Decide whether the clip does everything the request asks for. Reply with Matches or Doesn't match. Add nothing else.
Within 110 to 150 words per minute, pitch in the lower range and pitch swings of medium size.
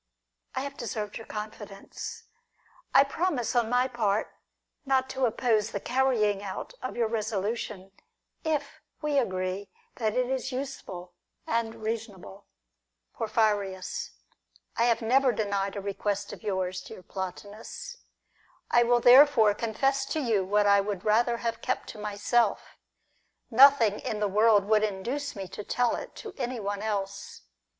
Doesn't match